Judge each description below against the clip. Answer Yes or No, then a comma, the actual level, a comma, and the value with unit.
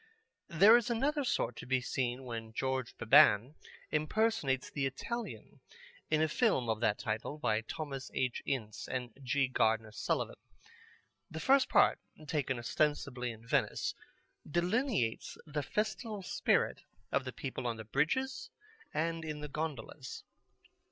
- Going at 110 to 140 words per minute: Yes, slow, 135 wpm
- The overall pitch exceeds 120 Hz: Yes, low, 135 Hz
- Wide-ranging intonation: Yes, wide, 5.9 semitones